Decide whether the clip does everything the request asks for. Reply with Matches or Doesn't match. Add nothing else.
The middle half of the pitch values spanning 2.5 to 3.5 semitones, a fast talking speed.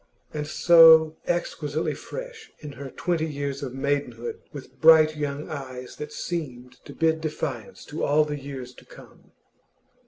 Doesn't match